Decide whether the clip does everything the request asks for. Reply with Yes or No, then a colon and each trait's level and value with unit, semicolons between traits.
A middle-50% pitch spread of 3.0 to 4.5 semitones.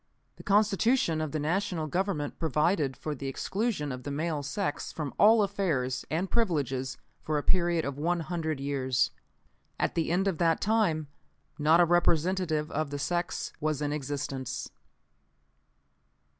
Yes: average, 3.9 semitones